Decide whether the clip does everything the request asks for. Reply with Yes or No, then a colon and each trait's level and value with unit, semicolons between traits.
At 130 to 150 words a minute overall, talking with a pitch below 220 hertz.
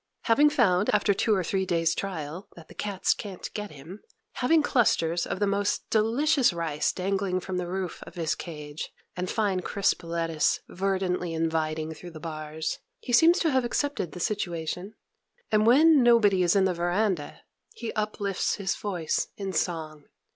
No: average, 170 wpm; medium, 185 Hz